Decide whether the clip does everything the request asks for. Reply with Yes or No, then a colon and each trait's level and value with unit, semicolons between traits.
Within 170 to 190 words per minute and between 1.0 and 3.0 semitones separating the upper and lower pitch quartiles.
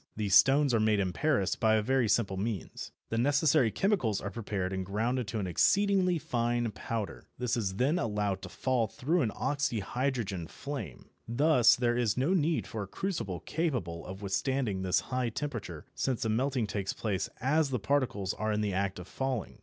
No: average, 185 wpm; average, 5.1 semitones